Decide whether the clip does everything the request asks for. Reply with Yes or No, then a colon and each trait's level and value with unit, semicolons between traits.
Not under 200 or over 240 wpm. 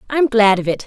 No: fast, 275 wpm